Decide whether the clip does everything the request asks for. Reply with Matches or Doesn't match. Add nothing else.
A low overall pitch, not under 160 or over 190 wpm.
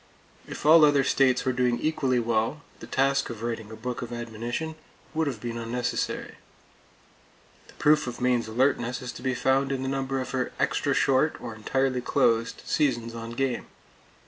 Matches